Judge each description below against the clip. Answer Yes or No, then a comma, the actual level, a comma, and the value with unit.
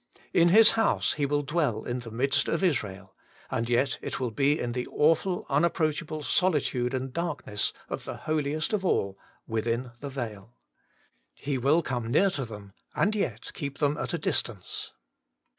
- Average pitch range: Yes, average, 4.8 semitones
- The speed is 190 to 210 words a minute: No, average, 175 wpm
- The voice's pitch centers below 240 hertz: Yes, medium, 140 Hz